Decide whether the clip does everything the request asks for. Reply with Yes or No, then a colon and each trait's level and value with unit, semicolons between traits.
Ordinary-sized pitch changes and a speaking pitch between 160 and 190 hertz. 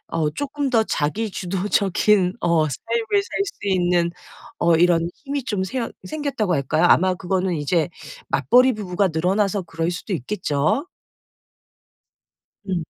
Yes: average, 4.6 semitones; medium, 185 Hz